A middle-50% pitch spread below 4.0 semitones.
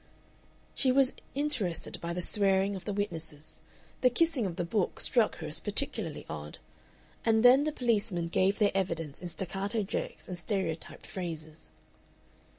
No: average, 4.9 semitones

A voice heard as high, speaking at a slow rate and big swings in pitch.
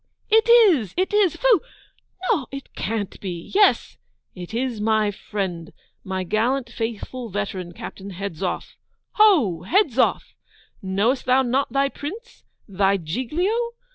Yes: high, 230 Hz; slow, 125 wpm; wide, 7.7 semitones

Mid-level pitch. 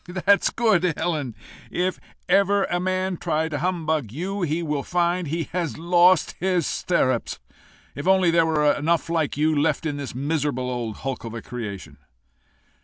Yes: medium, 160 Hz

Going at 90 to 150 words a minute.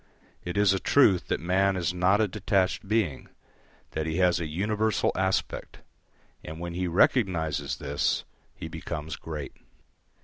Yes: average, 145 wpm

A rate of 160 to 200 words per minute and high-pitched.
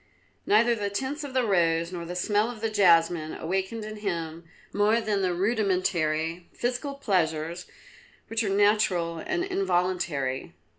No: average, 145 wpm; high, 195 Hz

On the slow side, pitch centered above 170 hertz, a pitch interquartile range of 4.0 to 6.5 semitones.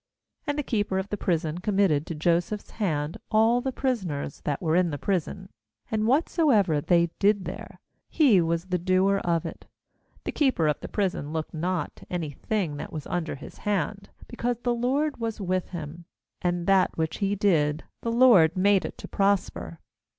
No: average, 180 wpm; medium, 185 Hz; average, 4.4 semitones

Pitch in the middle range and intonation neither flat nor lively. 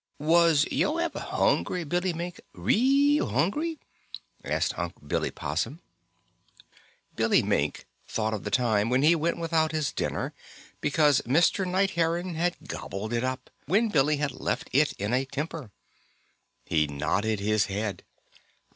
No: medium, 150 Hz; wide, 7.7 semitones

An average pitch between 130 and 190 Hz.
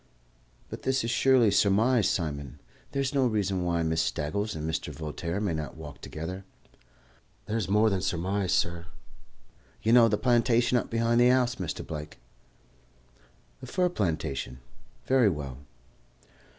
No: low, 100 Hz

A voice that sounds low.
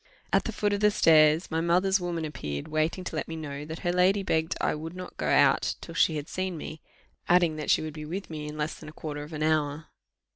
No: medium, 160 Hz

